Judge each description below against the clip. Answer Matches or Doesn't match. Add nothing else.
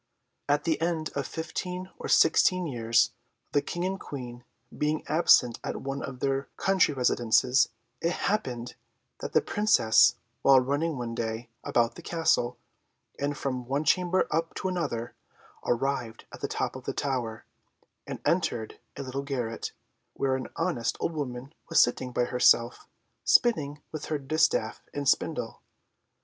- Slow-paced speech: Doesn't match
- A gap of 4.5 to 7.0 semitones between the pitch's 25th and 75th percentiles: Matches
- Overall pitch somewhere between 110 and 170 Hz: Matches